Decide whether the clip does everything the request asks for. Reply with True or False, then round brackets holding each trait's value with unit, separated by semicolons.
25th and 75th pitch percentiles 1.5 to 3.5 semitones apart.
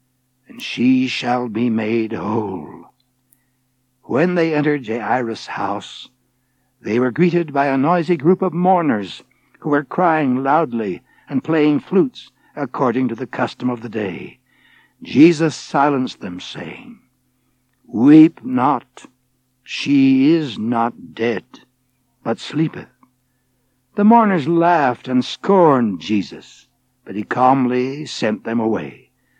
False (5.3 semitones)